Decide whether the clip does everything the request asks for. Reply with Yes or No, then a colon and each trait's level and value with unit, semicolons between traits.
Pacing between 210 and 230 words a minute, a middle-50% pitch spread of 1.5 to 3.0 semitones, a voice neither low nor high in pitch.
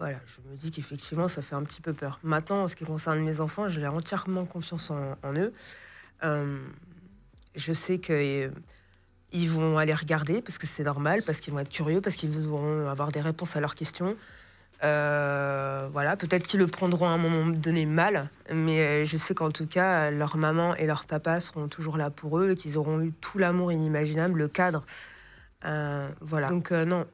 No: average, 200 wpm; average, 2.7 semitones; medium, 155 Hz